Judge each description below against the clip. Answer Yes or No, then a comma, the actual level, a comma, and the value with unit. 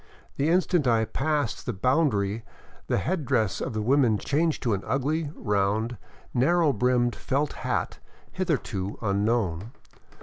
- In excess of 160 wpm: No, average, 140 wpm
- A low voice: Yes, low, 125 Hz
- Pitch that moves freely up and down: Yes, wide, 5.8 semitones